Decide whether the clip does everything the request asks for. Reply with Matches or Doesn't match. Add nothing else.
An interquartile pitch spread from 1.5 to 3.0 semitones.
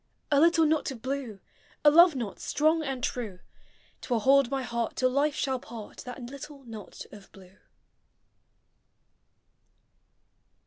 Doesn't match